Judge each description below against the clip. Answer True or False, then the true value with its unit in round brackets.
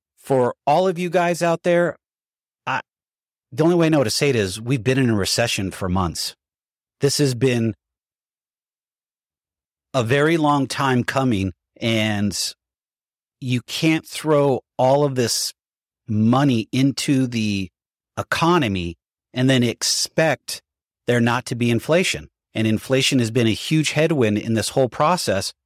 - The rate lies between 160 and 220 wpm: False (145 wpm)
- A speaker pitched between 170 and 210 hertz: False (125 Hz)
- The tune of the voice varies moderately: True (4.9 semitones)